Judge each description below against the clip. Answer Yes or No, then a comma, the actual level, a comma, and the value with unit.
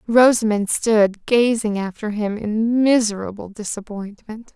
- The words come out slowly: Yes, slow, 105 wpm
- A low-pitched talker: No, high, 215 Hz